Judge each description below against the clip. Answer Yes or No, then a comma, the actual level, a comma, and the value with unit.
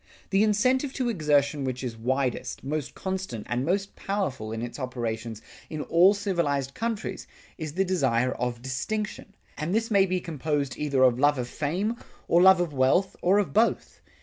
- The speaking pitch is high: No, medium, 150 Hz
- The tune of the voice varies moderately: No, wide, 7.0 semitones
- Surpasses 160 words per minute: Yes, average, 175 wpm